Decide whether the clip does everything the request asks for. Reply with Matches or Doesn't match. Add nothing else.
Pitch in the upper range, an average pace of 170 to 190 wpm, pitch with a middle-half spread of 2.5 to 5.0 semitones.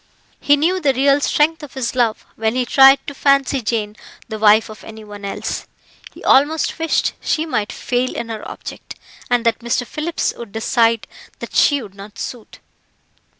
Matches